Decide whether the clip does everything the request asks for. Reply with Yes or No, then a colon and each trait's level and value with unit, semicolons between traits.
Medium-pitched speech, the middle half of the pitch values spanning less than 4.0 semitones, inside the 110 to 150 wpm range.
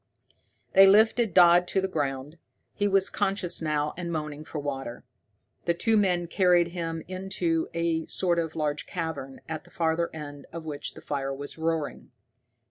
No: medium, 165 Hz; average, 3.1 semitones; average, 165 wpm